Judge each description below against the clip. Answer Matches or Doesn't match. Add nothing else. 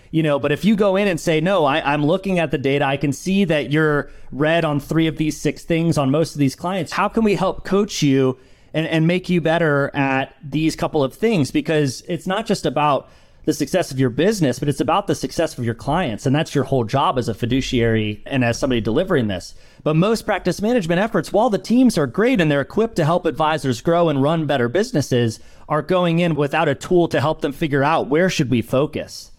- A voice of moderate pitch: Matches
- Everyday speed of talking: Doesn't match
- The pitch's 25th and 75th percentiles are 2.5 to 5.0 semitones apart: Matches